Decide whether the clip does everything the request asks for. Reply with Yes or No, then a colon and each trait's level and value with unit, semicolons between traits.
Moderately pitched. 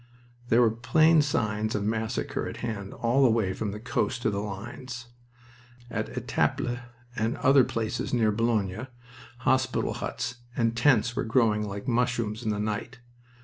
No: low, 115 Hz